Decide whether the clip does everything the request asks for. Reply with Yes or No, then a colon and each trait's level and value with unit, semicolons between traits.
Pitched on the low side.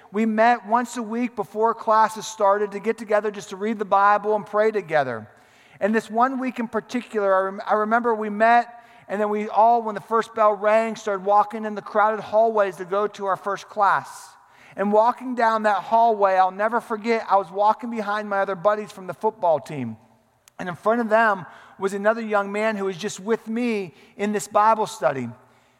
No: high, 210 Hz